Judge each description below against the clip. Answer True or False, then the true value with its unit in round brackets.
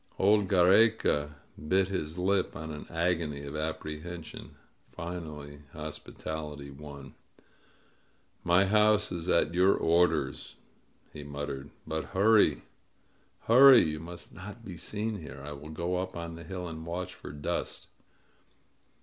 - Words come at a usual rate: False (130 wpm)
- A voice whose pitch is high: False (85 Hz)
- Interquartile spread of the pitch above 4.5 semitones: False (3.7 semitones)